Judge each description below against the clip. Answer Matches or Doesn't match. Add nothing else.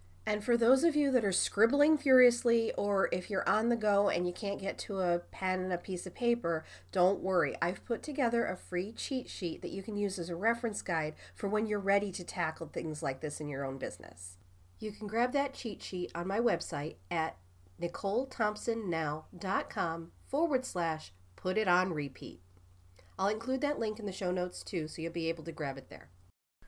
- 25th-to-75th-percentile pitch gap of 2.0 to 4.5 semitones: Doesn't match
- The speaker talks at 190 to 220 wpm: Matches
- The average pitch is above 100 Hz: Matches